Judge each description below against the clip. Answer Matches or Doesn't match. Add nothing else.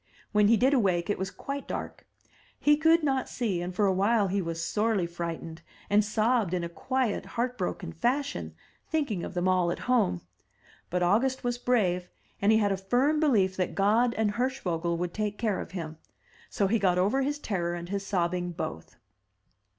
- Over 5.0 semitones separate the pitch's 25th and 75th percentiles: Matches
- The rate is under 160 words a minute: Doesn't match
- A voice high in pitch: Matches